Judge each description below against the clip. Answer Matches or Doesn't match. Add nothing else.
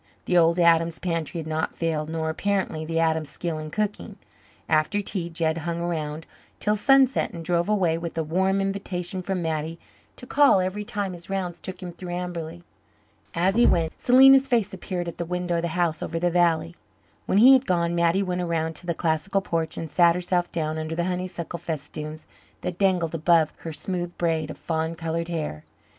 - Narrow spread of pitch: Matches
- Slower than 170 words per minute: Doesn't match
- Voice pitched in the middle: Matches